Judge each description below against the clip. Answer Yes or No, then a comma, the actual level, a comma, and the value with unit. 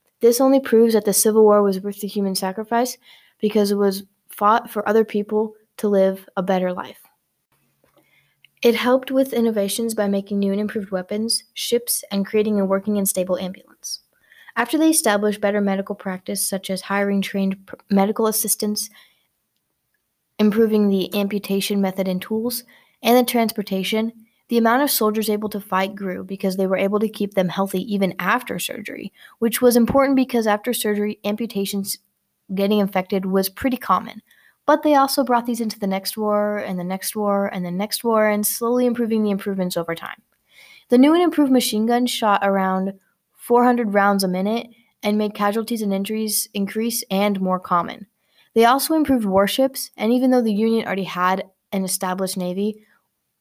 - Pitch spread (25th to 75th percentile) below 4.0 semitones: Yes, average, 2.8 semitones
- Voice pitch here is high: Yes, high, 210 Hz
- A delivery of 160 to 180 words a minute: Yes, average, 175 wpm